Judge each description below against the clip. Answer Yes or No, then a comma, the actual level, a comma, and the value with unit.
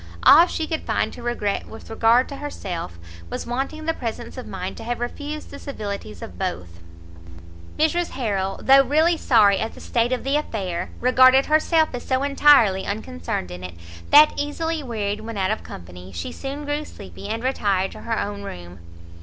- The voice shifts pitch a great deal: Yes, wide, 6.9 semitones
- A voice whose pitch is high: Yes, high, 235 Hz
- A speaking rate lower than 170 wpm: No, average, 185 wpm